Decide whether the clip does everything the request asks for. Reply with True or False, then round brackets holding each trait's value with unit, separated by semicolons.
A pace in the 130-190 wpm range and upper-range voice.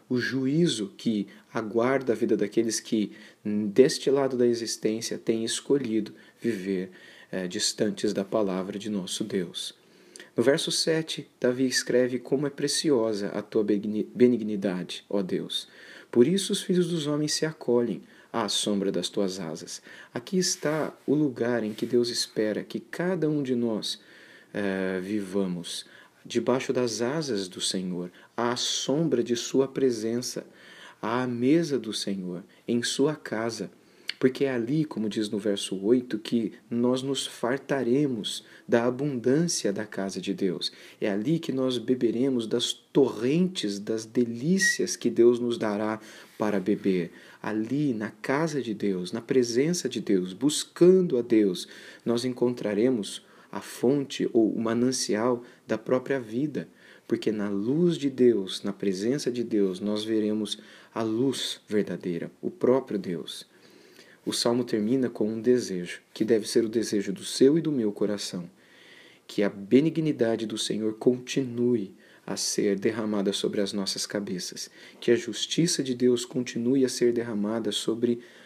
False (145 wpm; 115 Hz)